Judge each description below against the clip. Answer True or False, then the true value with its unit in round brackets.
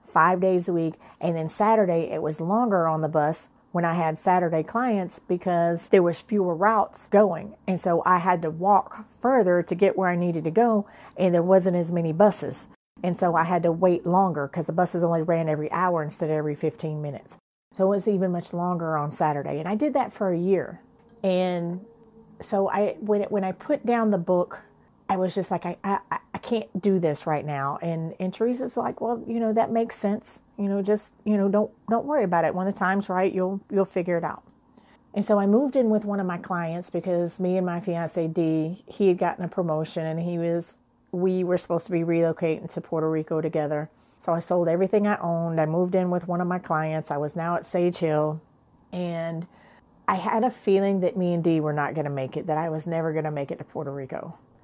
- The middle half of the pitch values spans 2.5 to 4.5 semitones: True (3.3 semitones)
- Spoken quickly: True (230 wpm)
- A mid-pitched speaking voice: True (180 Hz)